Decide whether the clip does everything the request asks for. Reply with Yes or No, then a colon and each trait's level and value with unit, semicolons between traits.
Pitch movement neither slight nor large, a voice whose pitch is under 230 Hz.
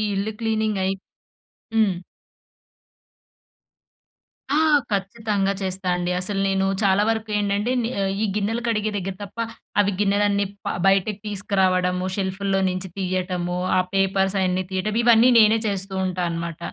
No: narrow, 2.0 semitones; high, 195 Hz